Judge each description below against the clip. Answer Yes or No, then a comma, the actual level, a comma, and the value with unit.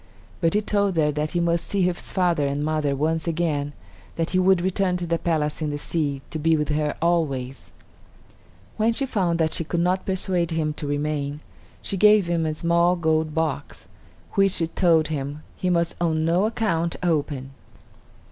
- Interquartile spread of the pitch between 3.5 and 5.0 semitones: No, average, 2.8 semitones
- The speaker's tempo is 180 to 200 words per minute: Yes, average, 185 wpm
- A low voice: No, medium, 165 Hz